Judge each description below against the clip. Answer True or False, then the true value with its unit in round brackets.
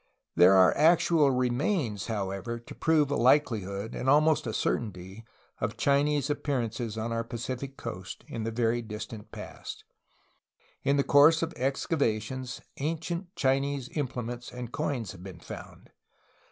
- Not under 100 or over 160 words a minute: True (140 wpm)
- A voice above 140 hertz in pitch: False (125 Hz)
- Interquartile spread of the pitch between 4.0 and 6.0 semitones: True (4.5 semitones)